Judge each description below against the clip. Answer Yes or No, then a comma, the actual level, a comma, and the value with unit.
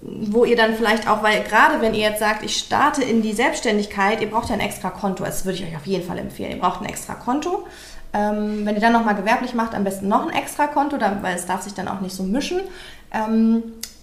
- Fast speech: Yes, fast, 240 wpm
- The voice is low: No, high, 220 Hz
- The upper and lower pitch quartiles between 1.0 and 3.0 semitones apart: Yes, narrow, 2.6 semitones